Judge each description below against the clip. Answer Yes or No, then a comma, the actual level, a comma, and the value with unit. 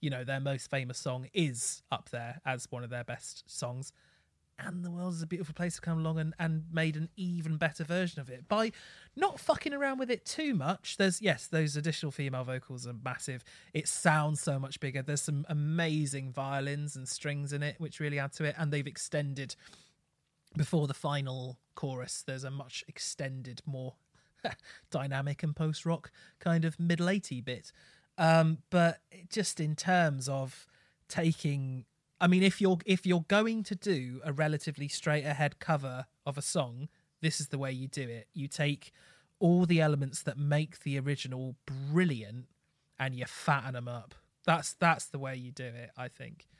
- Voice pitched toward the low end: No, medium, 150 Hz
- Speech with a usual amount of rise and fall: Yes, average, 3.7 semitones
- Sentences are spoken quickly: No, average, 185 wpm